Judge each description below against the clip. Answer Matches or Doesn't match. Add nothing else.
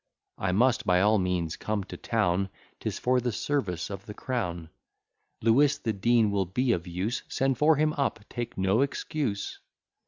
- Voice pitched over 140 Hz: Doesn't match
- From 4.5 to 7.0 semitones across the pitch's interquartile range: Matches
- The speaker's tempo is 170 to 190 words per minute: Matches